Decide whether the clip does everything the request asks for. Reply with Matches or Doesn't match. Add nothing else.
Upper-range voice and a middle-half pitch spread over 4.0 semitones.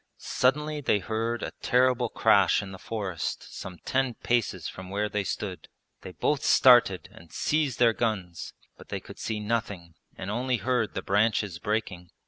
Doesn't match